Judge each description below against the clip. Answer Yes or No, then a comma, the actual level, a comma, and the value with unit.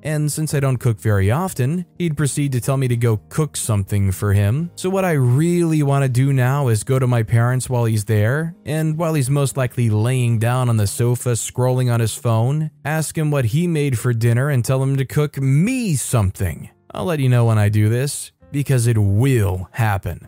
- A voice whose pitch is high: No, low, 125 Hz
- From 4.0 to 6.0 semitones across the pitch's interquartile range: Yes, average, 4.4 semitones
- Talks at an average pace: No, fast, 220 wpm